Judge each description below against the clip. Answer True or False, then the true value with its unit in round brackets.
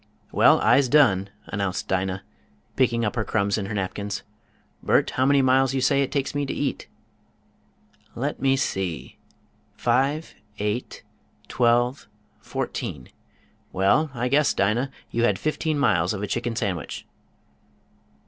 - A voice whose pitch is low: True (120 Hz)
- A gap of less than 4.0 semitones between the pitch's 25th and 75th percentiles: False (5.2 semitones)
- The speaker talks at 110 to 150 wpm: True (140 wpm)